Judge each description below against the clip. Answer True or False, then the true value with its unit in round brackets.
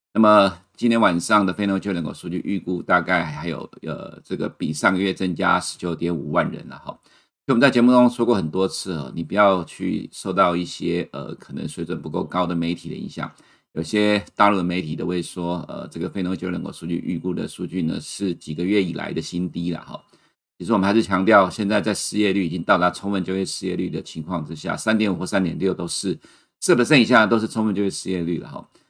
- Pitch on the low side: True (95 Hz)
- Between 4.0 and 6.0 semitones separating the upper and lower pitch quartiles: False (2.8 semitones)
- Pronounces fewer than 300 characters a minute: False (345 characters per minute)